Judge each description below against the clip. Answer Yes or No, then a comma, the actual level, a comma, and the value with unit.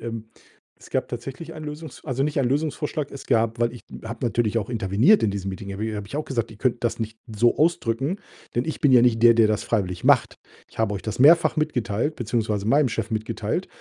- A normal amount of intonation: Yes, average, 4.3 semitones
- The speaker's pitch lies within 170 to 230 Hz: No, low, 115 Hz